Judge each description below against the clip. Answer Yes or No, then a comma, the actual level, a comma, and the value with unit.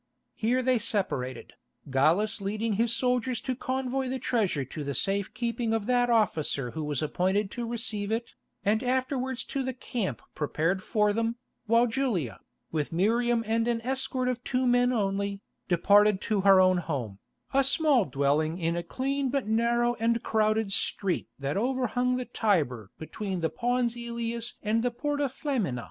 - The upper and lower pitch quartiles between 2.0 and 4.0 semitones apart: No, average, 4.8 semitones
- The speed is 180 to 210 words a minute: No, average, 165 wpm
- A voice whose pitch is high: Yes, high, 225 Hz